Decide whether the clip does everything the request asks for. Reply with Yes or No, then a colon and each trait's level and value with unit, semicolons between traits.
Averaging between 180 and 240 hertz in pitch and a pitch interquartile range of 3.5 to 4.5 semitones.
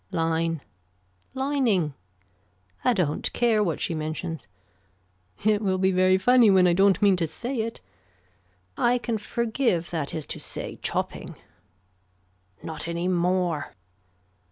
No: medium, 185 Hz; average, 5.1 semitones